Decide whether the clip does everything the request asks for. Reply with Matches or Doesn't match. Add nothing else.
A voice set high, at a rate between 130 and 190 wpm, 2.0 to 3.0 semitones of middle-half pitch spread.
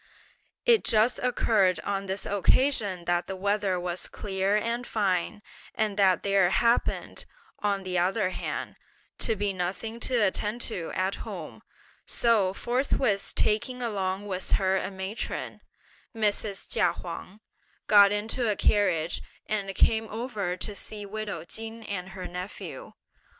Matches